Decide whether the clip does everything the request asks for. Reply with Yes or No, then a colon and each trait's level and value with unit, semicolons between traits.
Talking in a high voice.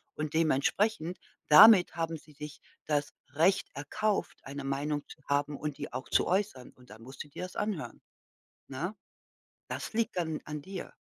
No: medium, 150 Hz